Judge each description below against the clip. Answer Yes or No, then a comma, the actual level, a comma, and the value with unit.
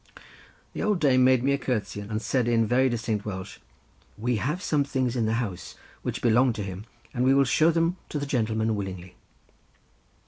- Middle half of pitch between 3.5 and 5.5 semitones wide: Yes, average, 3.8 semitones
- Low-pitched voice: Yes, low, 120 Hz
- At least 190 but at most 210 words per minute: Yes, average, 195 wpm